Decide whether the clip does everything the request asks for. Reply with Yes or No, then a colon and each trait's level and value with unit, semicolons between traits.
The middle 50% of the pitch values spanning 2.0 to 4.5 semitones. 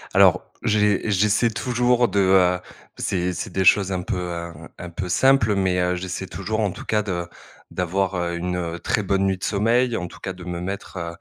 Yes: average, 2.8 semitones